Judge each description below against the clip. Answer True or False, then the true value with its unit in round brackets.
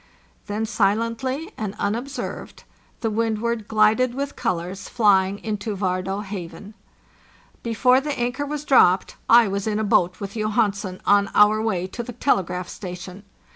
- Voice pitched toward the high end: True (215 Hz)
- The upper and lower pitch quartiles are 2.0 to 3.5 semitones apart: True (3.1 semitones)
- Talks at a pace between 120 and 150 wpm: True (140 wpm)